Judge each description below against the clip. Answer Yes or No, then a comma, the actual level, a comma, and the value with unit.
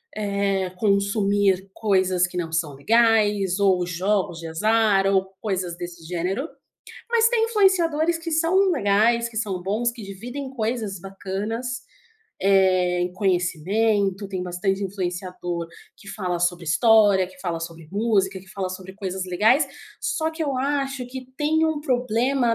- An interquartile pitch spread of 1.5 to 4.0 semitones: No, average, 4.5 semitones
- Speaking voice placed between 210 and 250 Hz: No, high, 200 Hz